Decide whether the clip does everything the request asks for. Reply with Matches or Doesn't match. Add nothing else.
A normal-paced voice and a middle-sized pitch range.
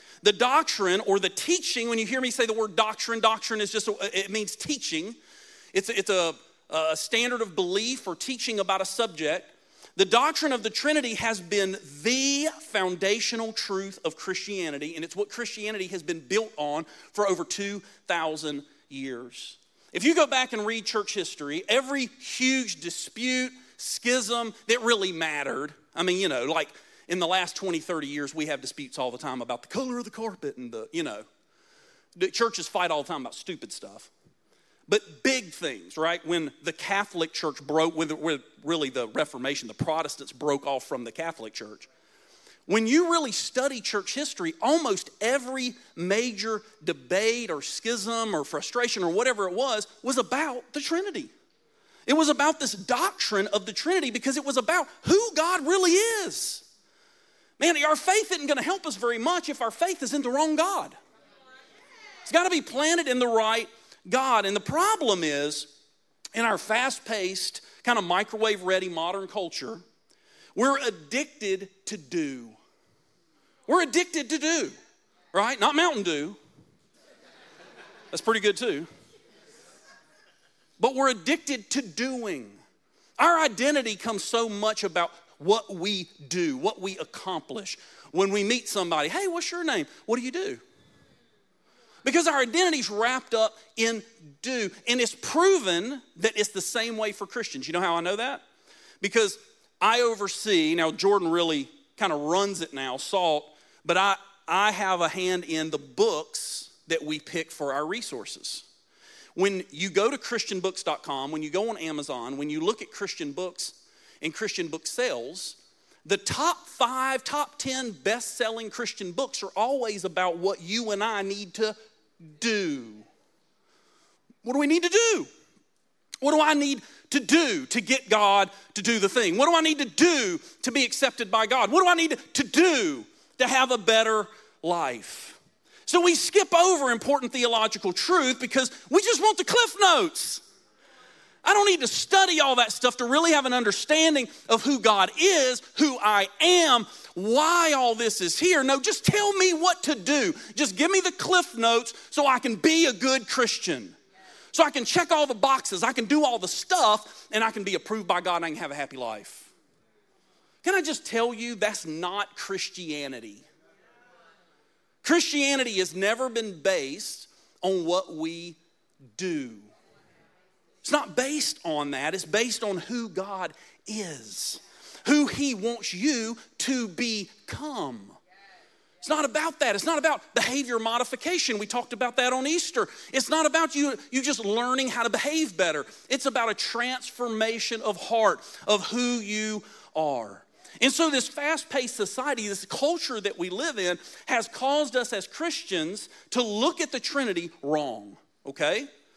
Doesn't match